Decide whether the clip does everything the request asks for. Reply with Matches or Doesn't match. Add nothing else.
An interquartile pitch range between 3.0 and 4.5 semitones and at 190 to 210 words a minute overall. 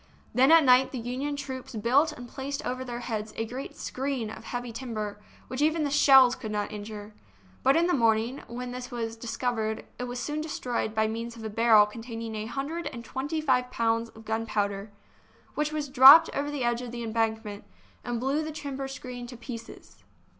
Matches